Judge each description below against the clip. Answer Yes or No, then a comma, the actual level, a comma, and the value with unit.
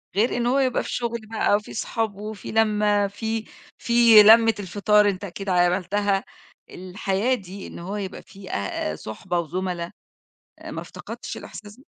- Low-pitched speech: No, high, 205 Hz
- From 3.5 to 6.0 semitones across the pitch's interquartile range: No, average, 2.9 semitones